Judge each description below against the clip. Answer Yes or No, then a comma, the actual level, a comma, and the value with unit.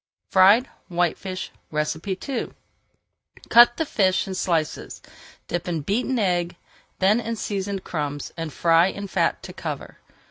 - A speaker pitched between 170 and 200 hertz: Yes, medium, 185 Hz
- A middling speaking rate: No, slow, 130 wpm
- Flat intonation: No, average, 3.4 semitones